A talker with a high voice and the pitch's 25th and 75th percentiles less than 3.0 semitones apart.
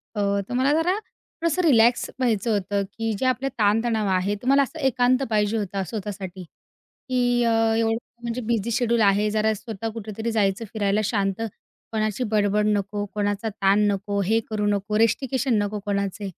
Yes: high, 215 Hz; narrow, 2.6 semitones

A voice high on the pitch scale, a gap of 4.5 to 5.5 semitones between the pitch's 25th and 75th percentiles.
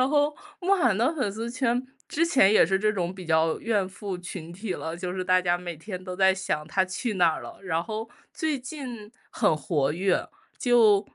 Yes: high, 195 Hz; average, 4.9 semitones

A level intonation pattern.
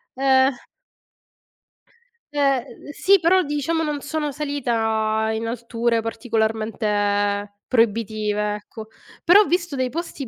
No: average, 5.0 semitones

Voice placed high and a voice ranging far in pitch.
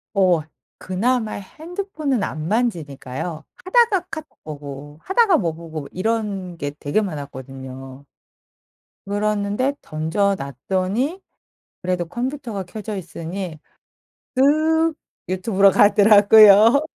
Yes: high, 200 Hz; wide, 7.4 semitones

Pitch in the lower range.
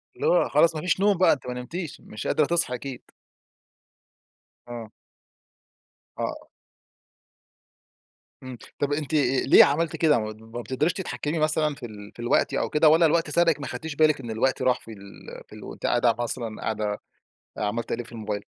Yes: low, 130 Hz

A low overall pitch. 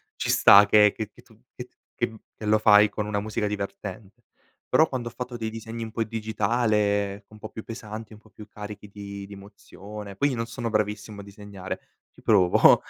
Yes: low, 105 Hz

